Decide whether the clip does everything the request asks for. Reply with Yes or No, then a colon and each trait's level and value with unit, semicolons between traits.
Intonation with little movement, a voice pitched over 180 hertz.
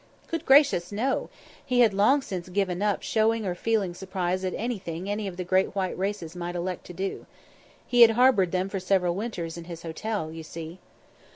No: average, 3.8 semitones; high, 190 Hz